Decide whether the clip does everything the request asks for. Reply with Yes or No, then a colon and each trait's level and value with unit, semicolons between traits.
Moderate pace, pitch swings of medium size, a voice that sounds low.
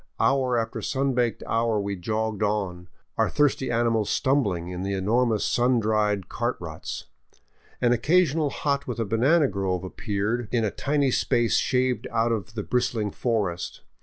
Yes: average, 160 wpm; average, 3.5 semitones; low, 115 Hz